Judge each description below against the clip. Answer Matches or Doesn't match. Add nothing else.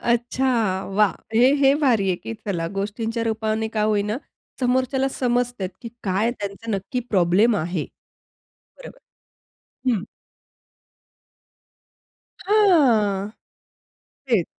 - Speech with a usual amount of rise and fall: Matches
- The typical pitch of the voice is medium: Doesn't match